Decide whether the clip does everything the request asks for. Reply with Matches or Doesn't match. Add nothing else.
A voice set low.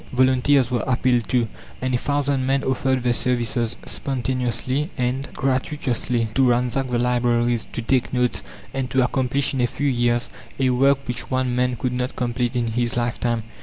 Matches